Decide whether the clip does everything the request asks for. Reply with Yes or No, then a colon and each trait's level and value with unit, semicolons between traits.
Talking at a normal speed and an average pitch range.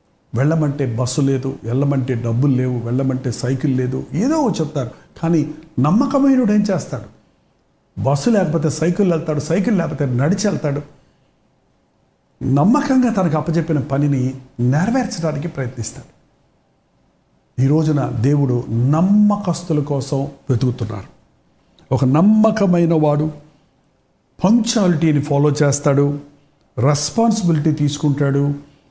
Yes: average, 85 wpm; average, 4.0 semitones